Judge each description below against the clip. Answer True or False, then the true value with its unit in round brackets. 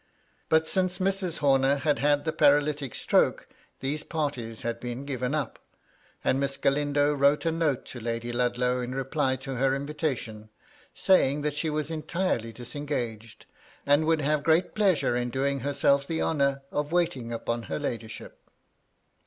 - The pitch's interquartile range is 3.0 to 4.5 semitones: True (3.4 semitones)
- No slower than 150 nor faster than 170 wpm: True (155 wpm)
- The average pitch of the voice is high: False (140 Hz)